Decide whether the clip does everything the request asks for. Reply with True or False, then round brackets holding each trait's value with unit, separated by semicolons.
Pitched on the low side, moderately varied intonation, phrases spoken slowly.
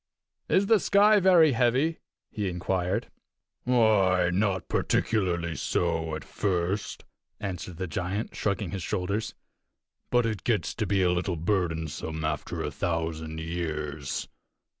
True (95 Hz; 4.7 semitones; 125 wpm)